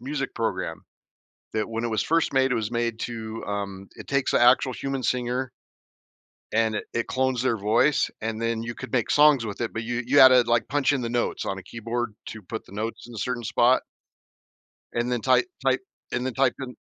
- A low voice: Yes, low, 120 Hz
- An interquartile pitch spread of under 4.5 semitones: Yes, narrow, 2.4 semitones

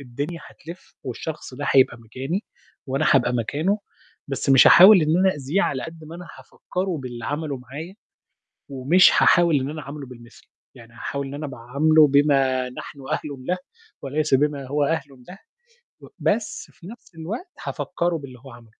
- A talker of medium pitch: Yes, medium, 145 Hz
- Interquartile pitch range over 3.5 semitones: Yes, average, 3.9 semitones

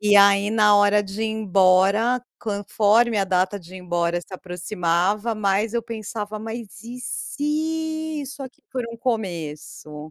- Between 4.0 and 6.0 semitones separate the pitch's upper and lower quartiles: No, average, 3.6 semitones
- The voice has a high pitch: Yes, high, 210 Hz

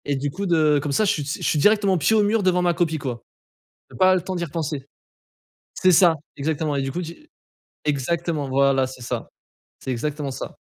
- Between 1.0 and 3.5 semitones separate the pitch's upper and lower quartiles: No, average, 4.5 semitones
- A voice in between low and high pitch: Yes, medium, 155 Hz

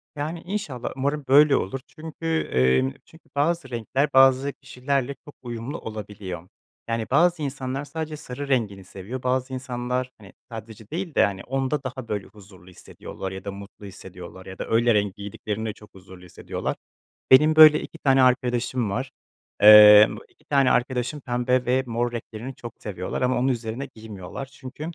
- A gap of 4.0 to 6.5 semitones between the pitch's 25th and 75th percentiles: Yes, average, 4.7 semitones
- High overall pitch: No, low, 125 Hz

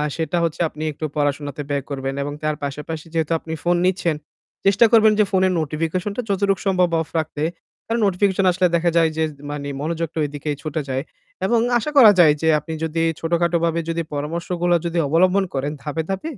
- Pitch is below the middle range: No, medium, 165 Hz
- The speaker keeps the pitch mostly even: No, average, 3.5 semitones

